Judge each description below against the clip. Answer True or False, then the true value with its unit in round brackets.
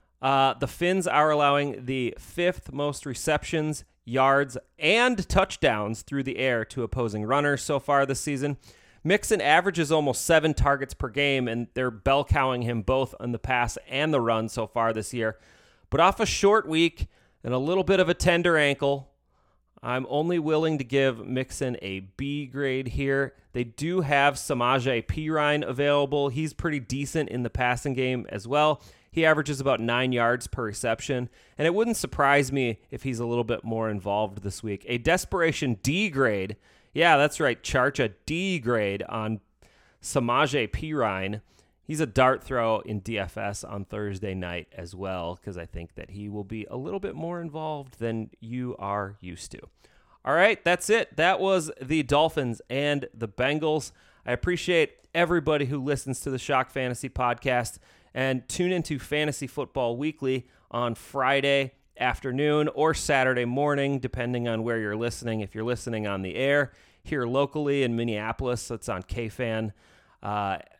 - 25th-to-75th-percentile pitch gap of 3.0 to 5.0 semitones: True (4.2 semitones)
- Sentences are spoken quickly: False (165 wpm)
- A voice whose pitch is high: False (130 Hz)